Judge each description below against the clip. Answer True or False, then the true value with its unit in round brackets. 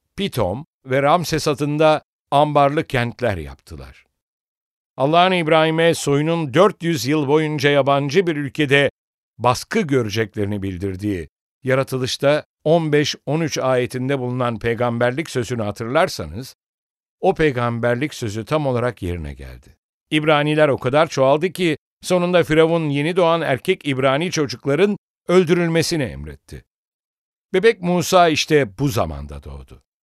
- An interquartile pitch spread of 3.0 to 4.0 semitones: False (5.0 semitones)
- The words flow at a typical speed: False (105 wpm)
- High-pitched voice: False (140 Hz)